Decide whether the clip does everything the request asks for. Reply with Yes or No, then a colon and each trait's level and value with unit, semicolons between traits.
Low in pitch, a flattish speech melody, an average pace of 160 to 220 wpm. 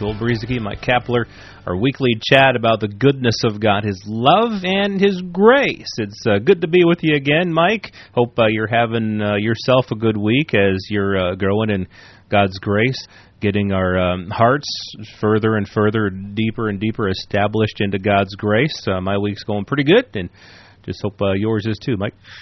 No: low, 110 Hz; average, 3.6 semitones; average, 185 wpm